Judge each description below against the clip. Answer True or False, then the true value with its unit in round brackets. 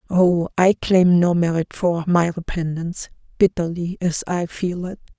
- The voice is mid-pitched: True (175 Hz)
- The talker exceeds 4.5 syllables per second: False (4.4 syllables/s)